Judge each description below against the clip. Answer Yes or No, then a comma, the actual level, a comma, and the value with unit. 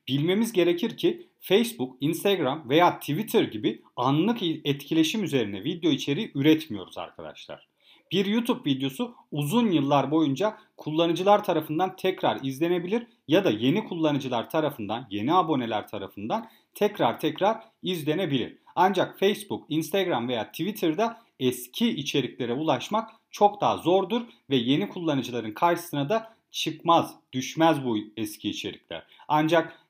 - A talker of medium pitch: Yes, medium, 165 Hz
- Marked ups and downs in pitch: Yes, wide, 6.1 semitones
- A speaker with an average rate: Yes, average, 115 wpm